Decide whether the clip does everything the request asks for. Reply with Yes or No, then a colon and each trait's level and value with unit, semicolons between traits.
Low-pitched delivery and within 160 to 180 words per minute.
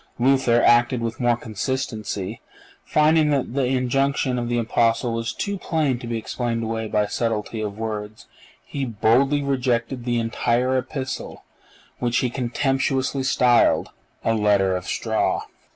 No: low, 120 Hz; average, 140 wpm